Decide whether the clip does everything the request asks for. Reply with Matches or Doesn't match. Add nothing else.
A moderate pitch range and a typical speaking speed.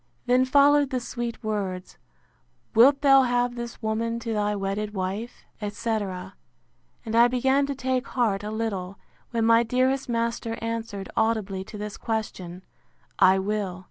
Matches